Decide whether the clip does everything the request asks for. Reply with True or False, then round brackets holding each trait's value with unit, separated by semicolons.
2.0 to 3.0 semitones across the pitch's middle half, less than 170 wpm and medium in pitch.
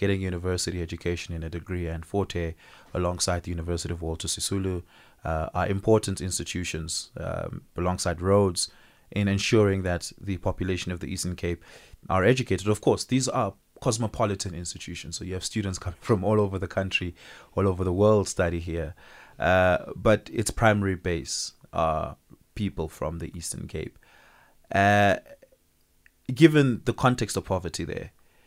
False (2.7 semitones; 150 wpm; 95 Hz)